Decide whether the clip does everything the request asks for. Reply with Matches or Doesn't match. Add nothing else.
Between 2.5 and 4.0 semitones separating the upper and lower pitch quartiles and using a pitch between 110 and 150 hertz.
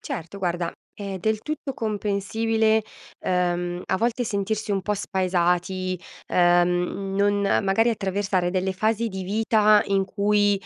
Doesn't match